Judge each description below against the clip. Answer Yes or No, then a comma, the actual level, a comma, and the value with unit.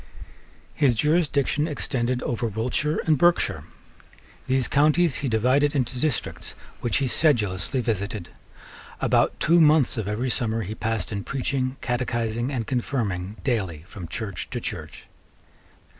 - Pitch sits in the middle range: No, low, 125 Hz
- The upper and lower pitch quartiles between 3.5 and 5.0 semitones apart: Yes, average, 4.4 semitones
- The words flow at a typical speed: No, slow, 130 wpm